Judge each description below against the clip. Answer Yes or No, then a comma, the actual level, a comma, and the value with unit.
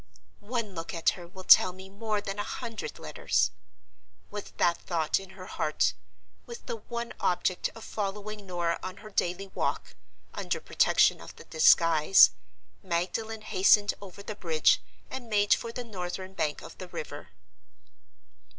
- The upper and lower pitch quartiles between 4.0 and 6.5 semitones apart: No, average, 3.4 semitones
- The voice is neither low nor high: No, high, 195 Hz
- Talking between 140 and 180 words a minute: Yes, average, 155 wpm